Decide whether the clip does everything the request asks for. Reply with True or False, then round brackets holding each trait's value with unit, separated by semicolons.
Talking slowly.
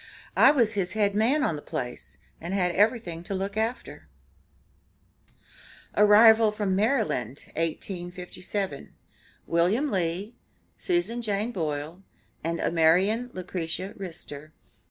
True (110 wpm)